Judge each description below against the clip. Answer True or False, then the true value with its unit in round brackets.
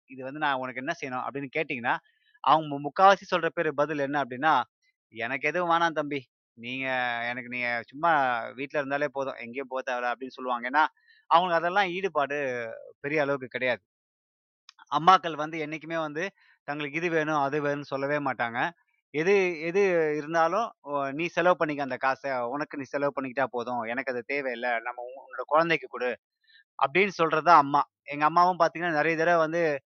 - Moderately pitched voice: True (145 Hz)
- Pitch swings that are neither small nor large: True (4.1 semitones)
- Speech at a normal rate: False (155 wpm)